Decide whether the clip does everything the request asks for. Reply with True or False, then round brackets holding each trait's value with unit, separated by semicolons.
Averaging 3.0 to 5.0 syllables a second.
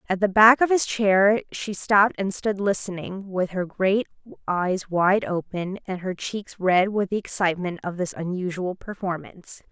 True (4.4 syllables/s)